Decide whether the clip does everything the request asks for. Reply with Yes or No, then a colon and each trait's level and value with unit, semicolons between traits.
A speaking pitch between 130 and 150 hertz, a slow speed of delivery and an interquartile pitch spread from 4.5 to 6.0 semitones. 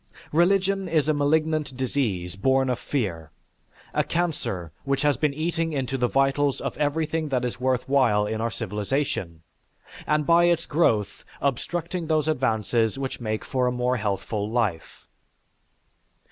No: low, 135 Hz; average, 145 wpm; wide, 5.5 semitones